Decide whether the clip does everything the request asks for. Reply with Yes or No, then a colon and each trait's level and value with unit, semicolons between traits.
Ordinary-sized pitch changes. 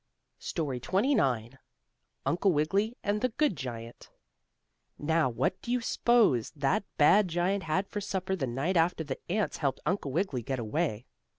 No: wide, 7.0 semitones